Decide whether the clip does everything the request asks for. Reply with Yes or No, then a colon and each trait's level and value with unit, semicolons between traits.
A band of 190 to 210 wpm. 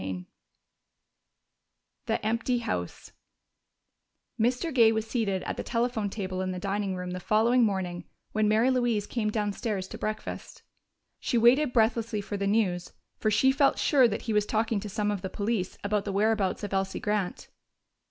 No: average, 170 wpm